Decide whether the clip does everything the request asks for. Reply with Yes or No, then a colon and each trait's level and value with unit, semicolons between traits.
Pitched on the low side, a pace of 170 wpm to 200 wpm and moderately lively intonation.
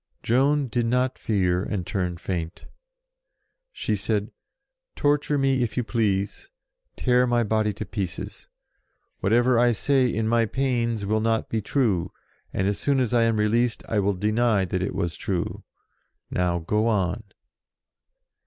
No: low, 110 Hz; average, 150 wpm; average, 3.8 semitones